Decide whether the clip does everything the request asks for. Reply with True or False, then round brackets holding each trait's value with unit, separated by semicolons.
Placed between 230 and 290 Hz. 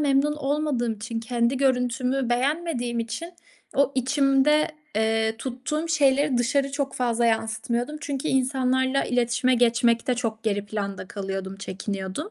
True (250 Hz)